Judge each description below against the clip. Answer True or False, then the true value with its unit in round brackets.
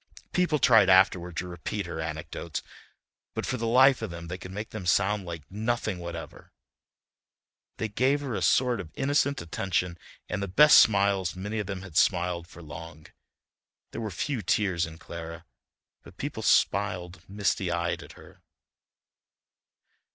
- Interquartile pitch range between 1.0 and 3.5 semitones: False (4.2 semitones)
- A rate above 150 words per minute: True (160 wpm)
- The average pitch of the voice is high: False (95 Hz)